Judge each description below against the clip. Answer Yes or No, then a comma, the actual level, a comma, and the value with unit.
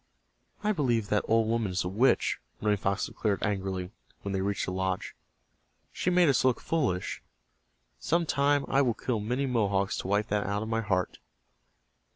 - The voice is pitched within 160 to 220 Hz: No, low, 105 Hz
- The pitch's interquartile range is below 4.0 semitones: No, average, 4.8 semitones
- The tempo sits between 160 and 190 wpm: Yes, average, 180 wpm